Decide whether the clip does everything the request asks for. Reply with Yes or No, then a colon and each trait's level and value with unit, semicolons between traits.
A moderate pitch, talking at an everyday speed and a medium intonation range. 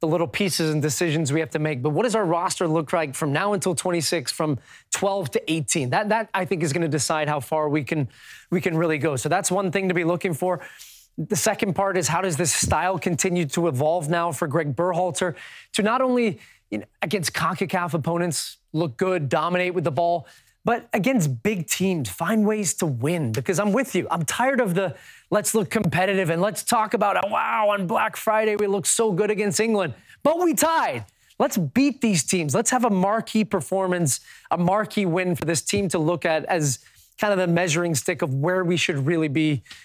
No: medium, 180 Hz; fast, 215 wpm; average, 3.7 semitones